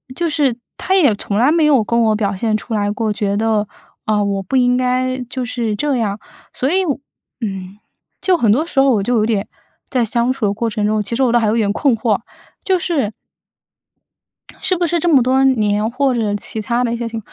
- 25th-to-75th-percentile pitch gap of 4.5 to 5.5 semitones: No, average, 4.0 semitones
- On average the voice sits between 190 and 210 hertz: No, high, 235 Hz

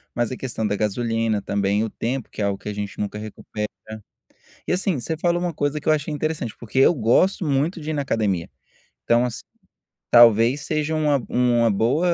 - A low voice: Yes, low, 120 Hz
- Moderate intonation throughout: No, wide, 5.8 semitones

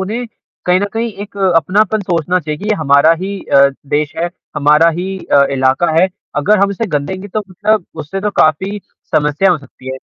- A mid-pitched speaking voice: Yes, medium, 180 Hz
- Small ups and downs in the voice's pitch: No, average, 5.1 semitones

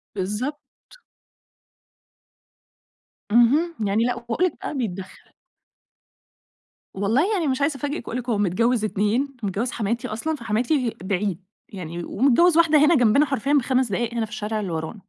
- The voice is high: Yes, high, 235 Hz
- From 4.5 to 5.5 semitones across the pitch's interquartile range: Yes, average, 5.2 semitones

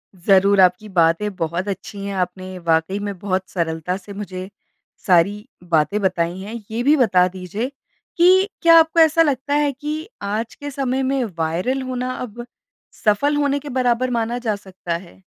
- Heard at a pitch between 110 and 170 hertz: No, high, 205 Hz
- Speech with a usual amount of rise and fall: No, wide, 6.1 semitones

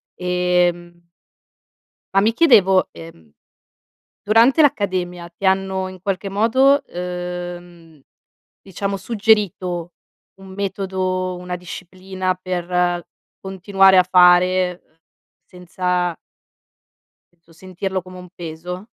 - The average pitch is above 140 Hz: Yes, medium, 185 Hz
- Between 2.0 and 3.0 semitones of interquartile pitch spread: No, narrow, 1.5 semitones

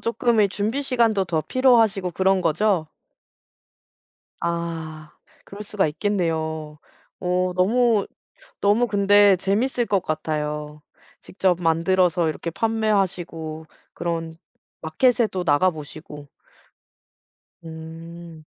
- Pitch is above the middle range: No, medium, 180 Hz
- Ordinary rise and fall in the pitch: Yes, average, 4.4 semitones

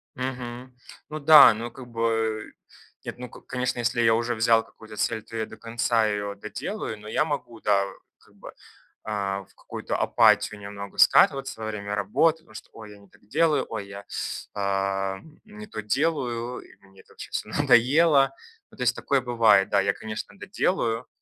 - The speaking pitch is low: Yes, low, 115 Hz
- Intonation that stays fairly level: No, average, 3.4 semitones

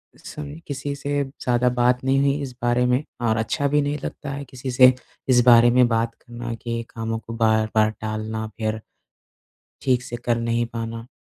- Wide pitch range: No, narrow, 2.6 semitones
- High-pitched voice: No, low, 120 Hz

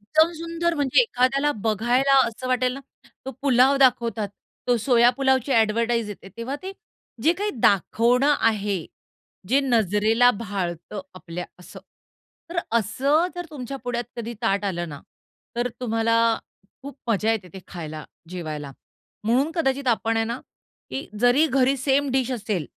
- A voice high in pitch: Yes, high, 240 Hz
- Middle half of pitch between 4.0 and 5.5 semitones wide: Yes, average, 4.3 semitones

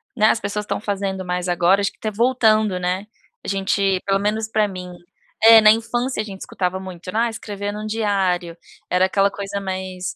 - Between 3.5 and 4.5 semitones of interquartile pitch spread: No, narrow, 2.4 semitones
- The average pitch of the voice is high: Yes, high, 200 Hz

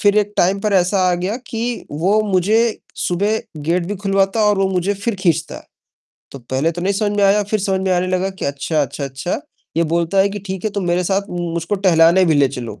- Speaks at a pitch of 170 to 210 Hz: Yes, high, 190 Hz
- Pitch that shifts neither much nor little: Yes, average, 3.0 semitones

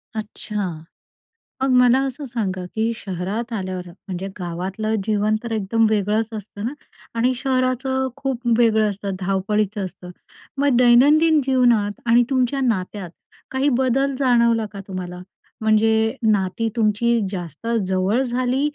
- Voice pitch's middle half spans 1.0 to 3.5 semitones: No, average, 4.2 semitones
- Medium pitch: No, high, 220 Hz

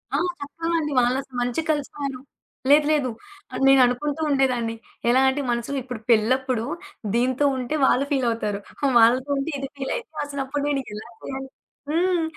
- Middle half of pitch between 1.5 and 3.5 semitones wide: Yes, average, 2.8 semitones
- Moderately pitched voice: No, very high, 270 Hz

